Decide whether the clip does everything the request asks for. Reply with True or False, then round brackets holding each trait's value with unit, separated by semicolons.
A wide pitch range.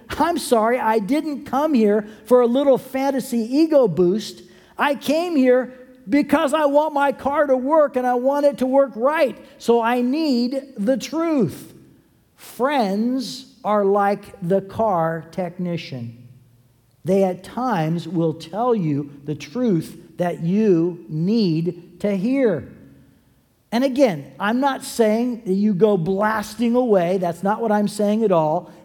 True (6.6 semitones)